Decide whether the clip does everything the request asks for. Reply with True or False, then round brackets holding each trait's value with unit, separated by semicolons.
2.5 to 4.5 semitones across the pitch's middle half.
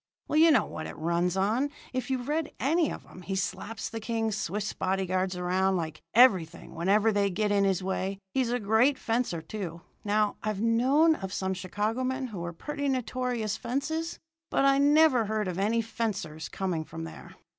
False (5.2 semitones)